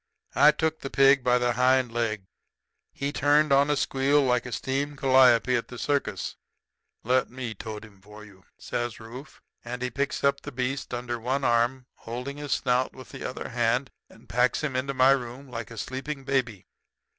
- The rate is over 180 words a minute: Yes, average, 190 wpm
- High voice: No, low, 130 Hz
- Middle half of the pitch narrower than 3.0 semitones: Yes, narrow, 2.5 semitones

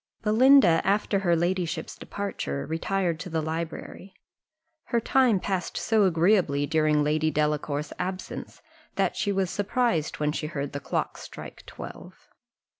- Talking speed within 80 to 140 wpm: Yes, slow, 135 wpm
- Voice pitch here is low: No, medium, 170 Hz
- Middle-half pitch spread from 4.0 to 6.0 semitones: Yes, average, 4.4 semitones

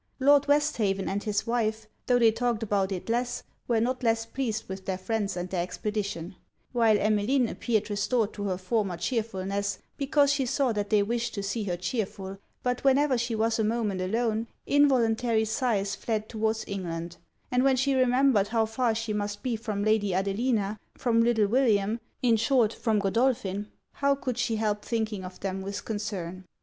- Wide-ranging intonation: No, average, 3.2 semitones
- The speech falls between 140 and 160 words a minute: No, average, 180 wpm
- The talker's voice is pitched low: No, high, 220 Hz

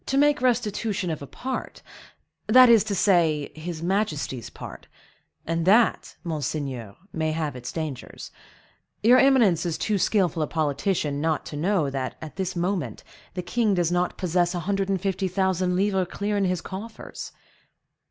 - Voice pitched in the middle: Yes, medium, 180 Hz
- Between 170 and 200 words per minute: No, average, 160 wpm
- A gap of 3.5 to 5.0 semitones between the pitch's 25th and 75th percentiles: Yes, average, 4.4 semitones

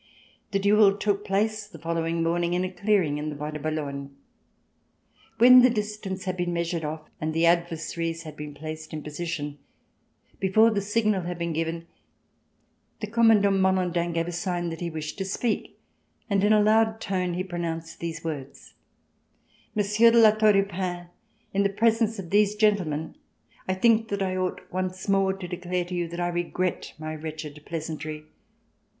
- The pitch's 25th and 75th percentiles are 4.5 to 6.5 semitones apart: No, average, 3.6 semitones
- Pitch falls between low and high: Yes, medium, 180 Hz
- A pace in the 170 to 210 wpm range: Yes, average, 175 wpm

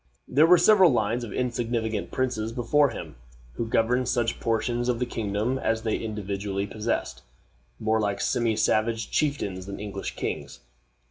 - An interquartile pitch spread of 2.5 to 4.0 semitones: Yes, average, 2.8 semitones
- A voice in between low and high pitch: No, low, 115 Hz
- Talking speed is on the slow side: No, average, 150 wpm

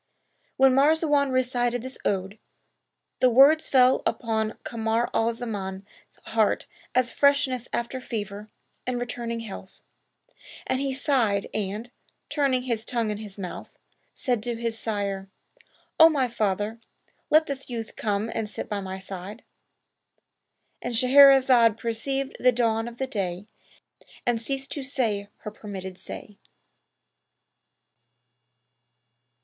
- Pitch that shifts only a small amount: No, average, 3.7 semitones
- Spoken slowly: Yes, slow, 120 wpm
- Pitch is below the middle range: No, high, 235 Hz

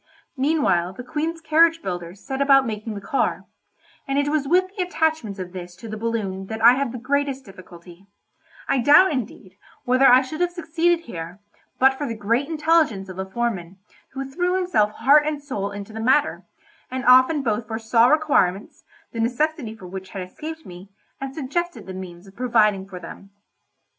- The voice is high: Yes, high, 245 Hz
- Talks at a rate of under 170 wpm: No, average, 185 wpm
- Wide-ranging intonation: Yes, wide, 7.2 semitones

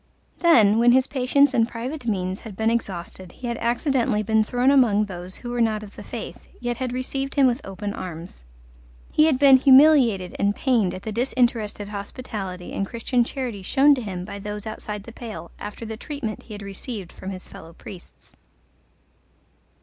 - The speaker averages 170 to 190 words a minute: Yes, average, 185 wpm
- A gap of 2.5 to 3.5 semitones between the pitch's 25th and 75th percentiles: No, average, 4.2 semitones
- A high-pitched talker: Yes, high, 225 Hz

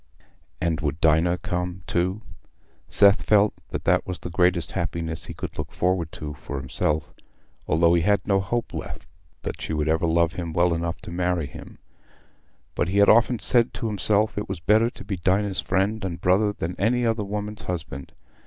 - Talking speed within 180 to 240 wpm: Yes, average, 190 wpm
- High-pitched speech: No, very low, 90 Hz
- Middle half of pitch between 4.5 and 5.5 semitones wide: No, average, 3.7 semitones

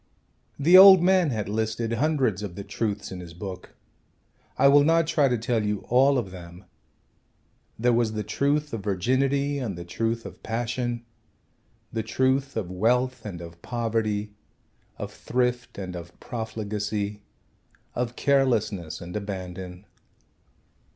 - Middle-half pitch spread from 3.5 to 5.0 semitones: Yes, average, 4.6 semitones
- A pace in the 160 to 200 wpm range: No, average, 145 wpm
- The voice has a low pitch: Yes, low, 115 Hz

